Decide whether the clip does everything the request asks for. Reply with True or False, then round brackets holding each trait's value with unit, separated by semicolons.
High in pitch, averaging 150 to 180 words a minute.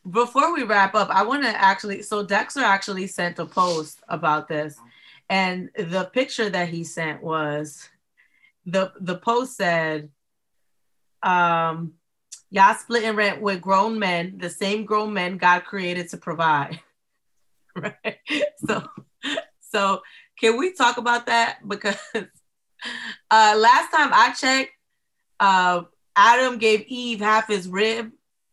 False (200 Hz; 135 wpm)